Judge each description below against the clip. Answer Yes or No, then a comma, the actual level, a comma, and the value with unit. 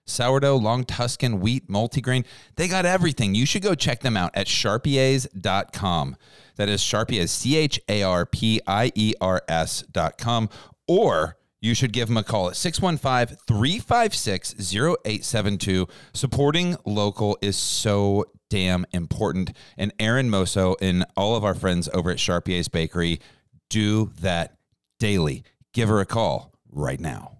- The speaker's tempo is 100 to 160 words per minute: Yes, average, 140 wpm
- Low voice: Yes, low, 110 Hz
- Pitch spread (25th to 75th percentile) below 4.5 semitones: No, average, 5.0 semitones